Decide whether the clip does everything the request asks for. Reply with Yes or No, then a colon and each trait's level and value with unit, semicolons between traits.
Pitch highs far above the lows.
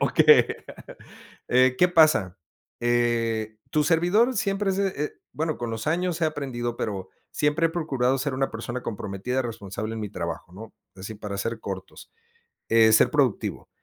Yes: wide, 6.0 semitones